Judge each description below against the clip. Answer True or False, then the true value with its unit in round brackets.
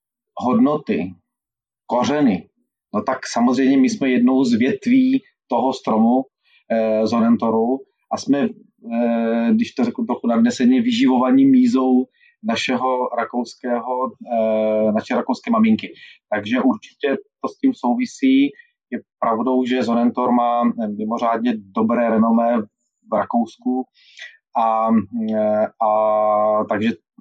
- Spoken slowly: True (110 wpm)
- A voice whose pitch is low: True (125 Hz)